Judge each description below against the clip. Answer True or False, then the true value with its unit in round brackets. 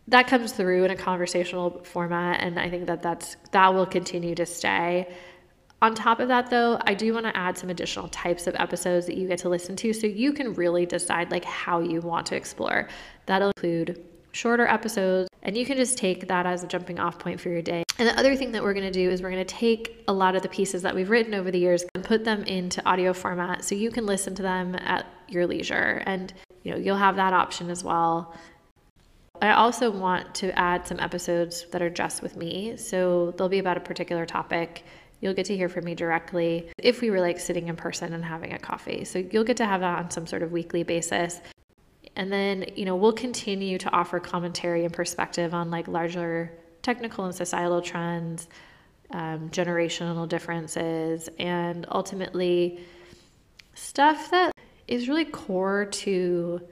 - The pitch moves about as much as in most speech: False (2.3 semitones)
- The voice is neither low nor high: True (180 Hz)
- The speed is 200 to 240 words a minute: True (205 wpm)